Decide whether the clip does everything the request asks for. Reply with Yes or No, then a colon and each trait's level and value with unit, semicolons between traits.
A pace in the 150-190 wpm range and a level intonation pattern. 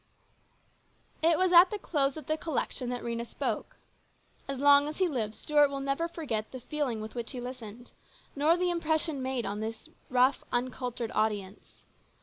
No: average, 170 wpm; average, 4.7 semitones